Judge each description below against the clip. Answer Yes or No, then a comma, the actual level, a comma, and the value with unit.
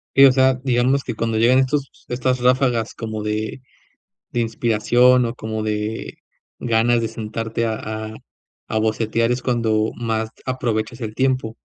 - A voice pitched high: No, low, 115 Hz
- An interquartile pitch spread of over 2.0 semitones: Yes, narrow, 2.4 semitones